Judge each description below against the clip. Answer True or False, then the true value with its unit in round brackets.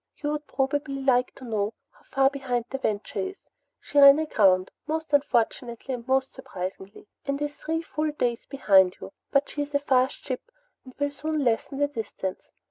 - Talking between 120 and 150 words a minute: False (185 wpm)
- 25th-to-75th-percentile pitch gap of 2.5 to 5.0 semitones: True (3.7 semitones)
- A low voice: False (270 Hz)